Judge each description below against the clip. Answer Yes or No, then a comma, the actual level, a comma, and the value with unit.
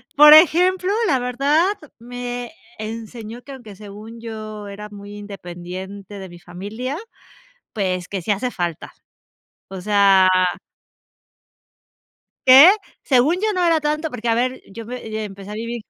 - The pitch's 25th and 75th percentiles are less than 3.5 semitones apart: No, average, 4.2 semitones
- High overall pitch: Yes, high, 220 Hz